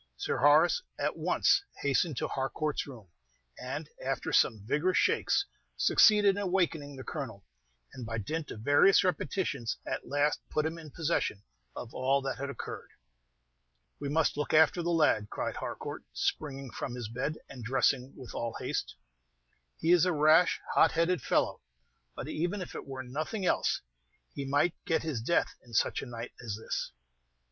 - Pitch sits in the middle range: Yes, medium, 145 Hz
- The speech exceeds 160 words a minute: Yes, average, 170 wpm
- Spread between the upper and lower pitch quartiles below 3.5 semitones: No, average, 4.4 semitones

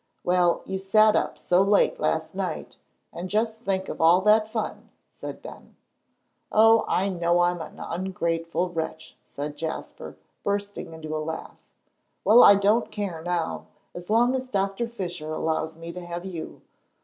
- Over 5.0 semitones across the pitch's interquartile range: No, average, 3.9 semitones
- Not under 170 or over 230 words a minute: No, average, 160 wpm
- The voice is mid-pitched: Yes, medium, 180 Hz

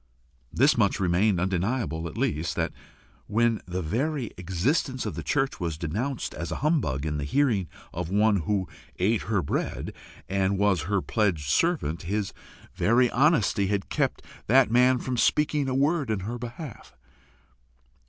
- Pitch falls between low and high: No, low, 105 Hz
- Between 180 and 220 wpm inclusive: No, average, 155 wpm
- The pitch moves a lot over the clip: Yes, wide, 6.3 semitones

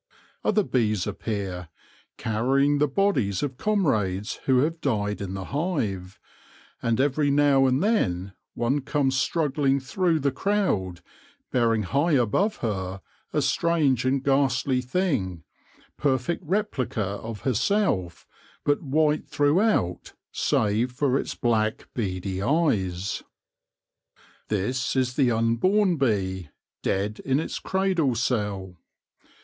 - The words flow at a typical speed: No, slow, 120 wpm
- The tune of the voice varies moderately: No, wide, 6.1 semitones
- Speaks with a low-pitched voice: Yes, low, 130 Hz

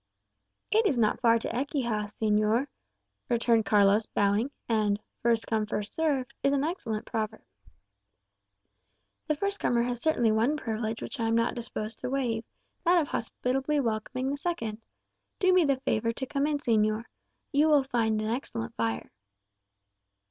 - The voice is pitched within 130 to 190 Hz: No, high, 235 Hz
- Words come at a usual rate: Yes, average, 155 wpm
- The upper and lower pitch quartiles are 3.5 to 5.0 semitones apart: Yes, average, 4.2 semitones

